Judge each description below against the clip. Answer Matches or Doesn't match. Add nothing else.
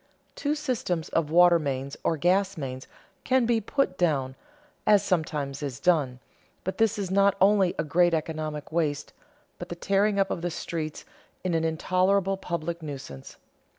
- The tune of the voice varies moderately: Matches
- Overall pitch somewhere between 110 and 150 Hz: Doesn't match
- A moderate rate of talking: Matches